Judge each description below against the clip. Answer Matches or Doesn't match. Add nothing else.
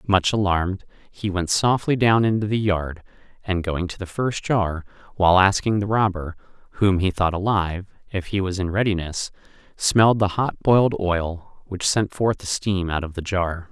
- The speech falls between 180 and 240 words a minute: Matches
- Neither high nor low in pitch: Doesn't match